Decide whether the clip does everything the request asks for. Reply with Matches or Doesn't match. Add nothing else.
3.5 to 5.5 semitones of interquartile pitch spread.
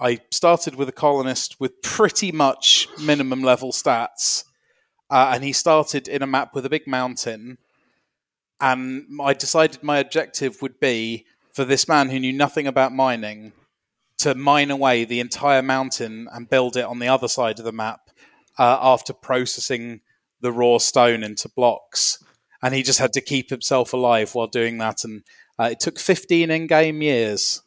Doesn't match